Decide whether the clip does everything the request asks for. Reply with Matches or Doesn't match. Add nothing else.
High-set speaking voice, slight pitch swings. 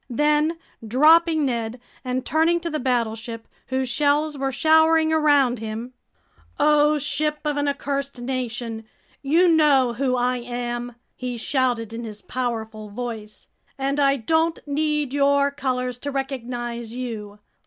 Doesn't match